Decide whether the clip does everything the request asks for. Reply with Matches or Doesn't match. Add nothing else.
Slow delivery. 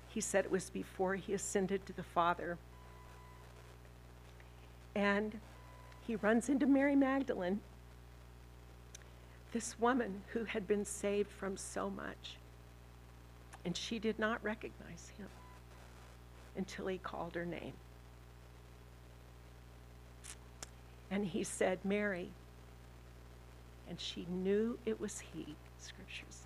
Matches